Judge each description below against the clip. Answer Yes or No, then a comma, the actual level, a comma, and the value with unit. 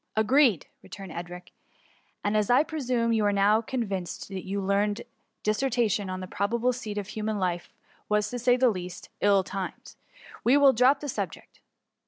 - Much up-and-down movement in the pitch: No, average, 4.0 semitones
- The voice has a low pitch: No, high, 210 Hz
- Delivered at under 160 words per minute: No, average, 200 wpm